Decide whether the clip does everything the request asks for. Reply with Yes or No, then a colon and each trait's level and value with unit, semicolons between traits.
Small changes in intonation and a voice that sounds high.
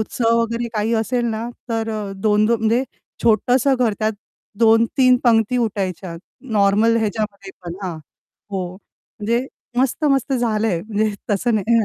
Yes: narrow, 2.2 semitones; high, 225 Hz